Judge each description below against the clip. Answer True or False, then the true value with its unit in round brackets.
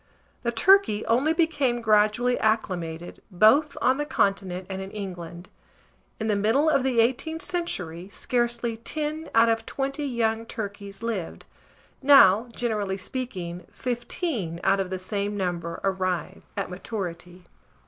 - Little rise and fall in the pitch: False (4.9 semitones)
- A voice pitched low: False (220 Hz)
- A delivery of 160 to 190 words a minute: False (135 wpm)